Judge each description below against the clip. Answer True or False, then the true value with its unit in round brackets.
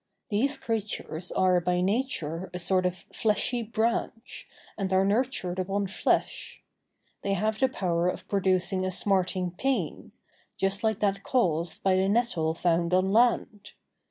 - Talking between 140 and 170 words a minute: True (145 wpm)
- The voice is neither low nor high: False (195 Hz)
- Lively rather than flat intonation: False (3.3 semitones)